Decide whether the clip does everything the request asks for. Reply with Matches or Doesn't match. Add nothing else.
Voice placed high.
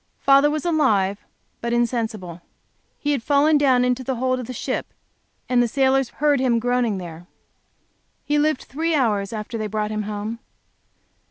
Matches